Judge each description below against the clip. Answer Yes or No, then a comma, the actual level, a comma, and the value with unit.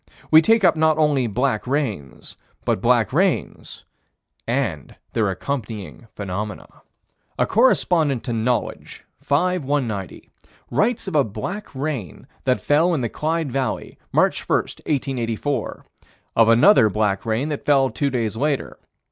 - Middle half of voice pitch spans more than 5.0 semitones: Yes, wide, 5.5 semitones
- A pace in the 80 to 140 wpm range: Yes, slow, 135 wpm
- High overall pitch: No, low, 135 Hz